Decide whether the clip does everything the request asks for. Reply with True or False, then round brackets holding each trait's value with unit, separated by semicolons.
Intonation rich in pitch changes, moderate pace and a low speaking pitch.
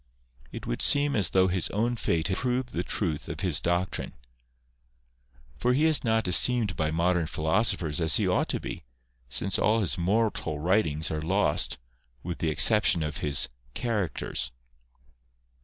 True (5.9 semitones; 165 wpm; 90 Hz)